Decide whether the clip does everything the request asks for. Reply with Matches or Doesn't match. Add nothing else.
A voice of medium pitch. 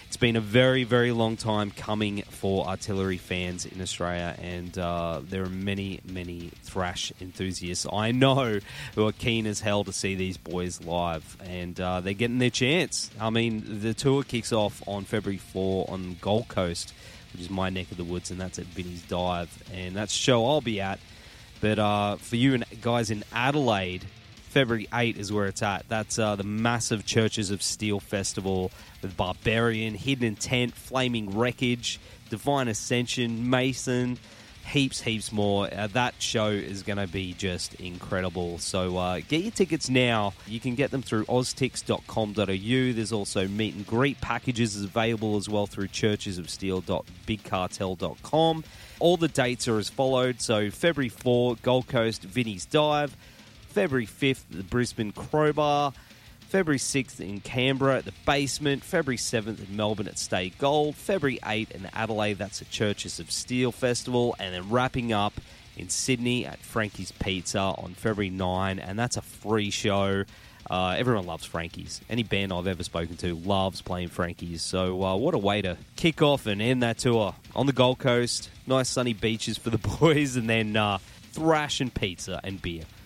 Doesn't match